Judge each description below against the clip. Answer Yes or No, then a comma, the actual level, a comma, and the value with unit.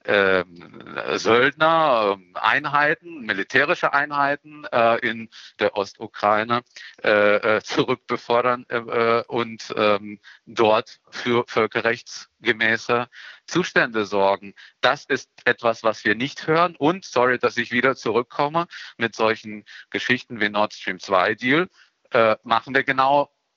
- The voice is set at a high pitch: No, low, 120 Hz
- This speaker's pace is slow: Yes, slow, 95 wpm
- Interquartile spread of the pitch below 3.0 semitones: No, average, 3.8 semitones